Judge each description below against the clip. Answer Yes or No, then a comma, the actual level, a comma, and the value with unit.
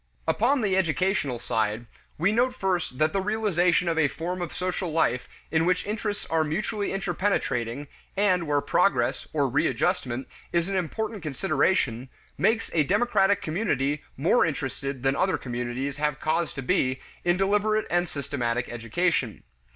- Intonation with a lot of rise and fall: Yes, wide, 6.0 semitones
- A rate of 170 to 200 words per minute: No, average, 150 wpm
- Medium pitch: Yes, medium, 165 Hz